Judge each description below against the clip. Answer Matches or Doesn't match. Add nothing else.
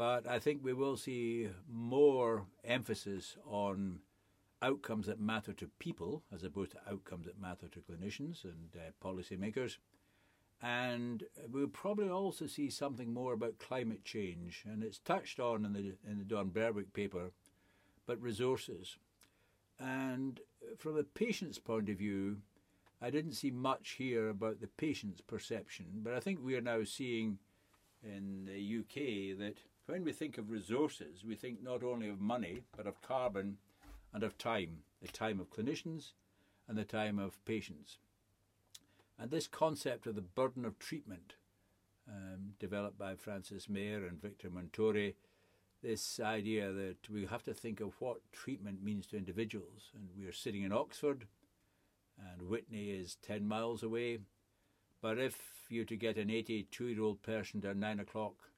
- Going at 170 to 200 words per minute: Doesn't match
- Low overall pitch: Matches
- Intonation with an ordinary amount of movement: Matches